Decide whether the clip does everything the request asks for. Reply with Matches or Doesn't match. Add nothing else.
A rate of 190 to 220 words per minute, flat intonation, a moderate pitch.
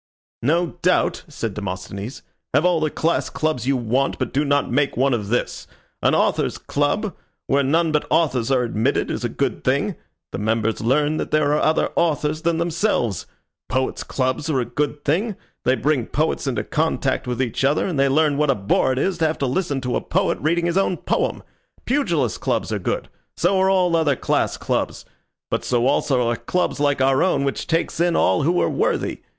Doesn't match